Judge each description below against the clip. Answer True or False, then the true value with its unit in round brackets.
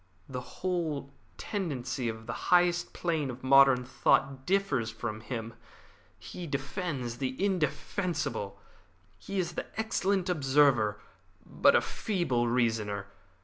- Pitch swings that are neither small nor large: False (6.6 semitones)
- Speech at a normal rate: False (115 wpm)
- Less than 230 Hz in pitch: True (135 Hz)